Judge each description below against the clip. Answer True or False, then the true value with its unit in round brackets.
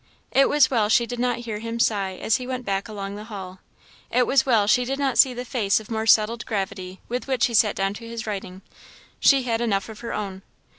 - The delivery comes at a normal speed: False (240 wpm)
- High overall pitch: True (225 Hz)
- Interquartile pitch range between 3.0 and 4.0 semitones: True (3.4 semitones)